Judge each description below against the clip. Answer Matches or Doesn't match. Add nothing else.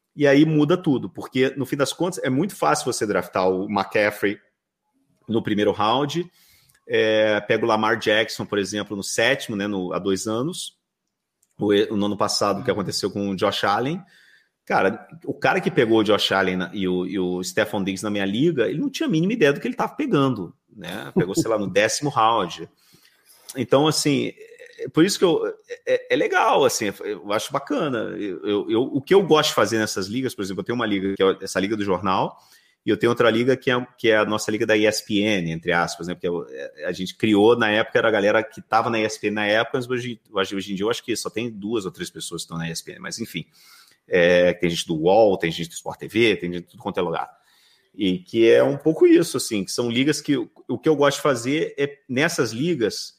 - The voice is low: Matches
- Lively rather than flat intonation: Matches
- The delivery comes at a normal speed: Doesn't match